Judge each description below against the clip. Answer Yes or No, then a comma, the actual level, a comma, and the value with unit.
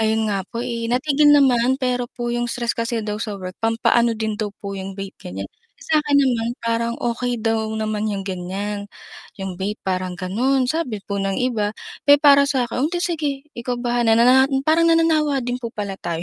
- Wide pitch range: No, average, 3.6 semitones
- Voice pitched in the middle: No, high, 235 Hz